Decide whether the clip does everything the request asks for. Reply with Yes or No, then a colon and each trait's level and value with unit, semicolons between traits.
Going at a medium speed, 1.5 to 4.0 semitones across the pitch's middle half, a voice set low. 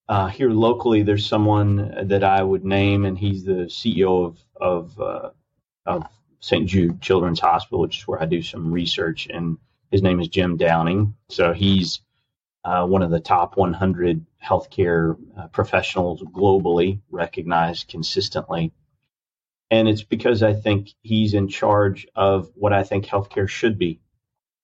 Yes: average, 150 wpm; average, 2.9 semitones; very low, 95 Hz